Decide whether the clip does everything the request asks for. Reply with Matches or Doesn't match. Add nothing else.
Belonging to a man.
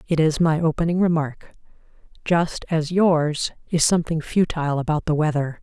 Doesn't match